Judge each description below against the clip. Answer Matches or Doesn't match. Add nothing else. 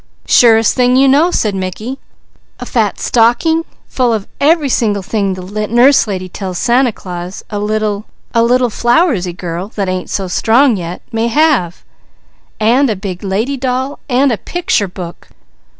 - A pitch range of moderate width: Matches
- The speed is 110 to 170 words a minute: Matches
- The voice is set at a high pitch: Matches